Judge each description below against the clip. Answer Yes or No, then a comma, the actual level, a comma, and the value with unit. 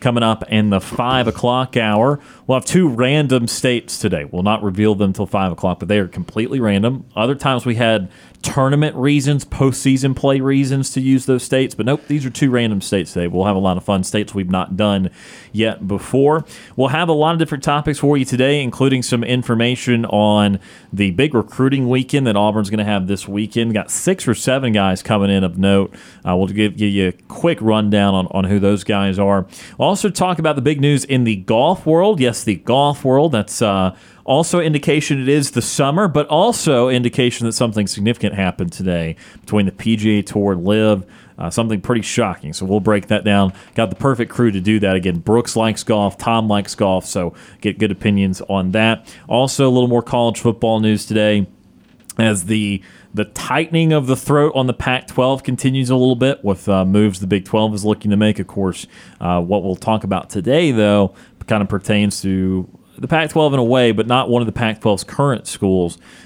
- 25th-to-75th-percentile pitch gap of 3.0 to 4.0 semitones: No, average, 4.7 semitones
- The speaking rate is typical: No, fast, 210 wpm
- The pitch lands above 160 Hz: No, low, 110 Hz